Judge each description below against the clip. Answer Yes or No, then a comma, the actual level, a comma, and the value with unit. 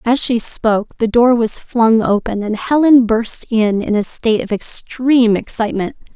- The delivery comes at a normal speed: Yes, average, 175 wpm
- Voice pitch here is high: Yes, high, 225 Hz